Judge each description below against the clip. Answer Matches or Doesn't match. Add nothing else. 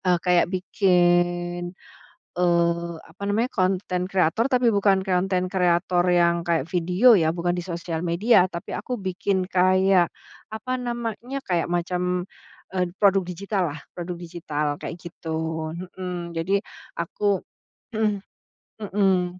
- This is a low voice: Doesn't match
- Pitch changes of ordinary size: Doesn't match